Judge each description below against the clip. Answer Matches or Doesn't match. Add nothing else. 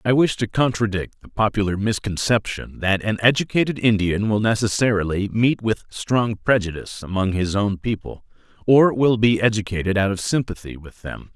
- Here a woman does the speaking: Doesn't match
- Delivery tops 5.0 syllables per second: Matches